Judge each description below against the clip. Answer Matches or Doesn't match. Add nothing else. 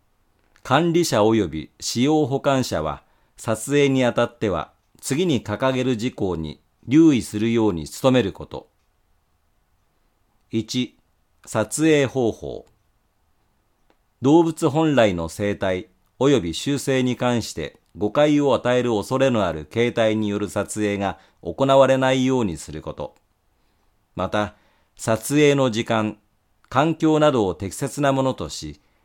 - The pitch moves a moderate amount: Doesn't match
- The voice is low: Matches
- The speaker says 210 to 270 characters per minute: Matches